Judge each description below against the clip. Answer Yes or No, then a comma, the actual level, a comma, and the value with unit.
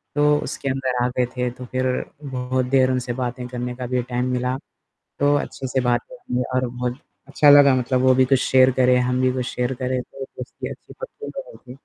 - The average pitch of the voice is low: Yes, low, 130 Hz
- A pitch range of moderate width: No, narrow, 1.0 semitones